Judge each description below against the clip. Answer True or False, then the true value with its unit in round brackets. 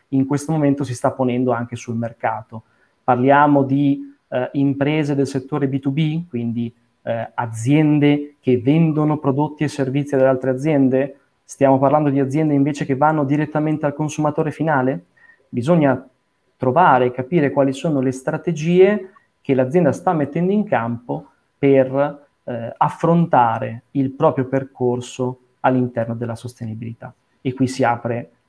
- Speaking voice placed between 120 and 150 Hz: True (140 Hz)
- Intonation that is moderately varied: True (3.0 semitones)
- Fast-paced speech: False (135 wpm)